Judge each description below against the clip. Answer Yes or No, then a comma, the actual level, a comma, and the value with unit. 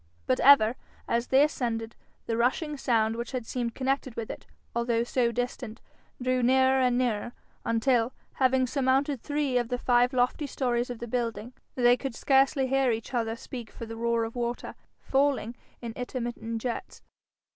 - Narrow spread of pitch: Yes, narrow, 2.1 semitones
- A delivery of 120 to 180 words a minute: Yes, average, 170 wpm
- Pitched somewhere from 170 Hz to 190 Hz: No, high, 245 Hz